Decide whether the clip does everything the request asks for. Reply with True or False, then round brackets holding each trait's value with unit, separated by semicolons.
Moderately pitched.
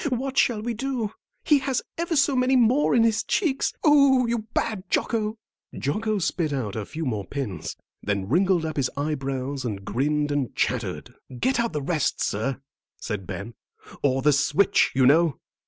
True (165 Hz)